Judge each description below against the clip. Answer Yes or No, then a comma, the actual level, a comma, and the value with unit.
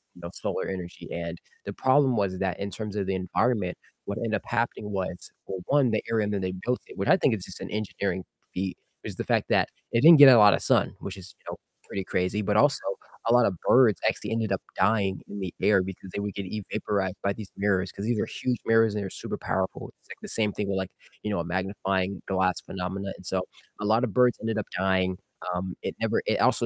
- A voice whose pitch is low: Yes, low, 100 Hz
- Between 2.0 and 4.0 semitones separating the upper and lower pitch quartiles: Yes, average, 2.8 semitones